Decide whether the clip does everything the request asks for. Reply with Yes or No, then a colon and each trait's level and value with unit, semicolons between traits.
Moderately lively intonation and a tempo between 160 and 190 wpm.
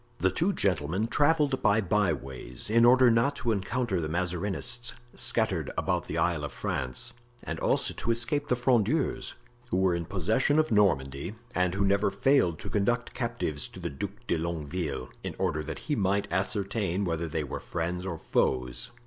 No: wide, 6.0 semitones; average, 175 wpm